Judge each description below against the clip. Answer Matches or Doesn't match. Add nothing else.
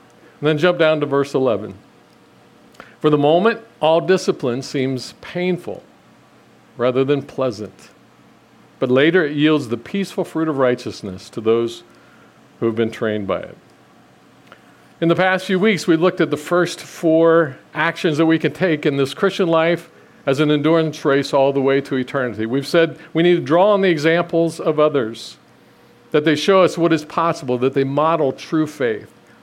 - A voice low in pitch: Doesn't match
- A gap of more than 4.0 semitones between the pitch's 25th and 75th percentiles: Doesn't match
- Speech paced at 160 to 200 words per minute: Matches